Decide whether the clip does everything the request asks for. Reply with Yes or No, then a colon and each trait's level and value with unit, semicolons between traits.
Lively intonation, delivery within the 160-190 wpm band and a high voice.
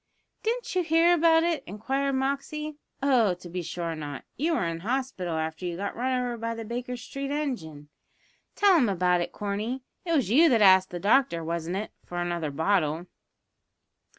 Yes: wide, 7.9 semitones; average, 180 wpm; high, 225 Hz